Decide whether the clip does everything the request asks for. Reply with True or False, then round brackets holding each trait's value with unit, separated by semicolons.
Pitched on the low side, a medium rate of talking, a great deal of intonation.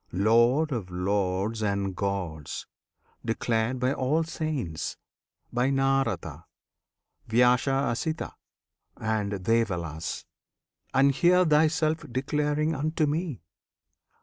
False (125 Hz; 95 wpm; 6.8 semitones)